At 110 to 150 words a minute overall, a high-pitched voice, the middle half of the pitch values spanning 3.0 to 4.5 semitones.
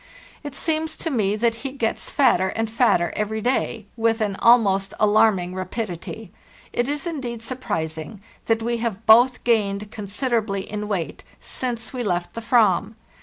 No: average, 160 wpm; high, 225 Hz; average, 3.4 semitones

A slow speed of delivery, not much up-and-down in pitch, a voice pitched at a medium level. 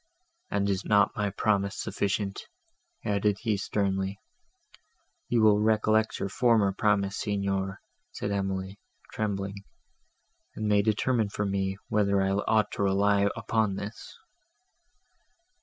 No: slow, 120 wpm; narrow, 1.4 semitones; low, 100 Hz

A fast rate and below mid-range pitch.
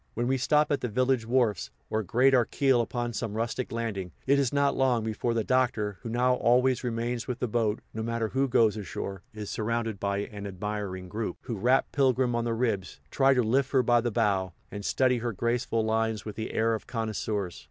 Yes: fast, 215 wpm; low, 115 Hz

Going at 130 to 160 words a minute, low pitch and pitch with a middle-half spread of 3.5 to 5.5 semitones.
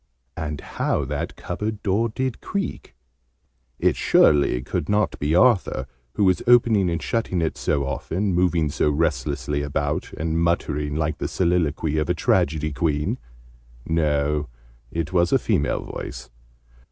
Yes: average, 140 wpm; very low, 80 Hz; average, 4.0 semitones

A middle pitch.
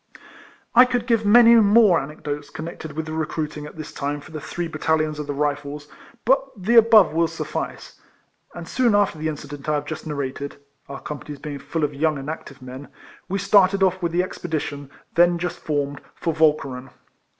Yes: medium, 155 Hz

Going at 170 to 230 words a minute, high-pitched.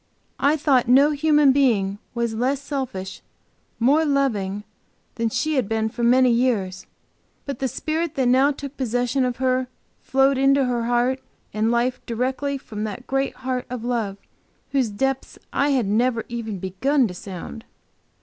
No: average, 160 wpm; very high, 250 Hz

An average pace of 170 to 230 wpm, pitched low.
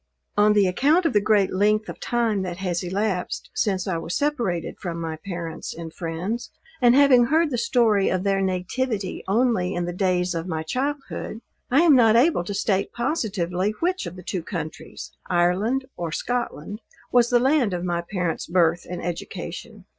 No: average, 180 wpm; high, 195 Hz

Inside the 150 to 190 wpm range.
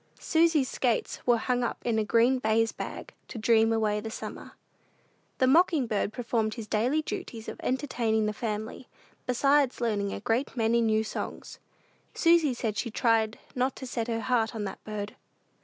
Yes: average, 175 wpm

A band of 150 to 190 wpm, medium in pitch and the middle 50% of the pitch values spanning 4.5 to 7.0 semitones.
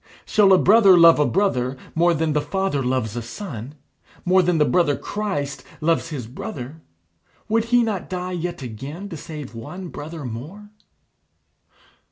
Yes: average, 160 wpm; medium, 165 Hz; wide, 5.6 semitones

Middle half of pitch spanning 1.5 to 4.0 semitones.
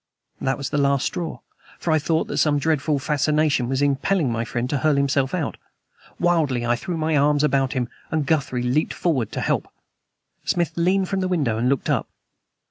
Yes: average, 3.2 semitones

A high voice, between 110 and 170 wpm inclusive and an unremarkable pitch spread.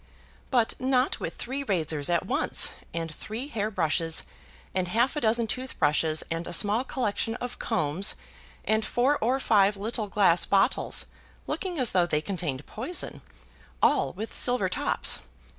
No: high, 210 Hz; average, 150 wpm; wide, 6.3 semitones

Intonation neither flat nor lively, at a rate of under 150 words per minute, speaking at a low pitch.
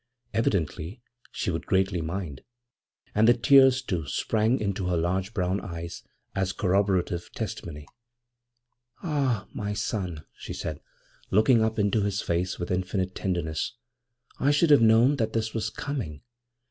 Yes: average, 4.2 semitones; average, 140 wpm; low, 100 Hz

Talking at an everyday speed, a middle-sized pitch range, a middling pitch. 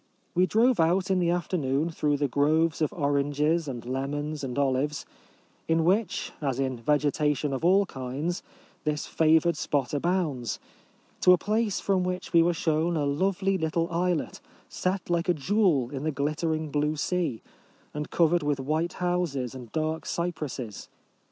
Yes: average, 160 wpm; average, 3.7 semitones; medium, 155 Hz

